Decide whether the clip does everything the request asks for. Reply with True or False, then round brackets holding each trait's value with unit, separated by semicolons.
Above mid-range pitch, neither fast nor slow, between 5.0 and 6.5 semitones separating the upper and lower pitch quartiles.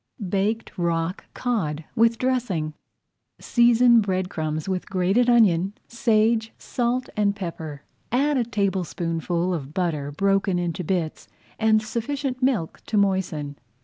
False (195 Hz; 120 wpm; 5.5 semitones)